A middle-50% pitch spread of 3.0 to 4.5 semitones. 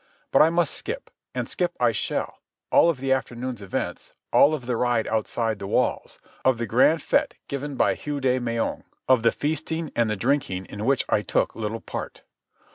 Yes: average, 4.2 semitones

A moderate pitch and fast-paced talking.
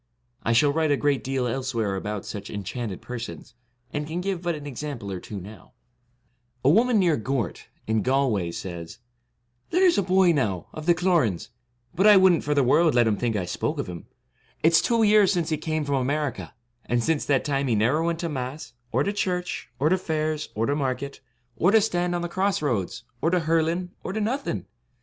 Yes: medium, 145 Hz; fast, 215 wpm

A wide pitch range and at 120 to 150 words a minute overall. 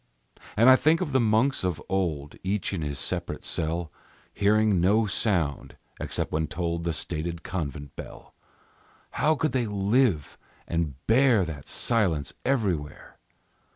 Yes: wide, 5.8 semitones; average, 140 wpm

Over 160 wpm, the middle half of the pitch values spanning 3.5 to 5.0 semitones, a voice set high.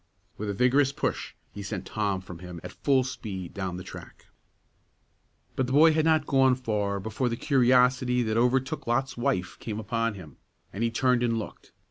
No: average, 185 wpm; average, 4.4 semitones; low, 115 Hz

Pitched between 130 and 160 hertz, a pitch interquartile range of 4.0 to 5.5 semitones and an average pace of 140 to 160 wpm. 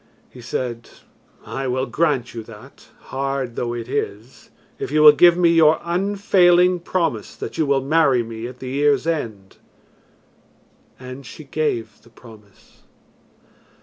Yes: low, 135 Hz; average, 5.2 semitones; average, 145 wpm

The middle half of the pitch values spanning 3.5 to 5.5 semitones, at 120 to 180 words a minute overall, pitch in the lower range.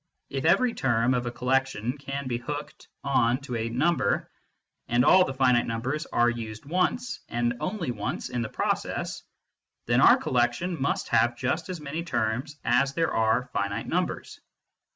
Yes: average, 4.0 semitones; average, 165 wpm; low, 125 Hz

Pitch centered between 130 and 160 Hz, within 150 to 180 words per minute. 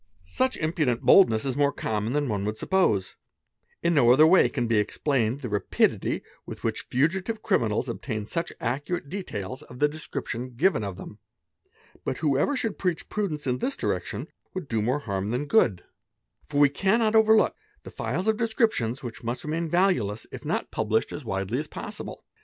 No: medium, 140 Hz; average, 190 wpm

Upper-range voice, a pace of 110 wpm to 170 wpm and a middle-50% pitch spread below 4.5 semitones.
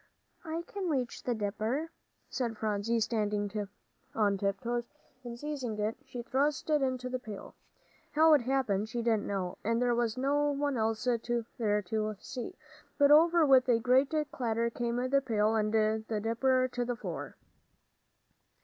Yes: high, 235 Hz; average, 160 wpm; average, 3.4 semitones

